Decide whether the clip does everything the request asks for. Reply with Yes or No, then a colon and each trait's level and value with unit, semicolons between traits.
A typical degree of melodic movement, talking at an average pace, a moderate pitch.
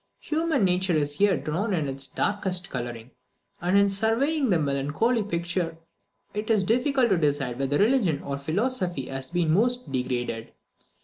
No: wide, 7.5 semitones; average, 150 wpm; medium, 180 Hz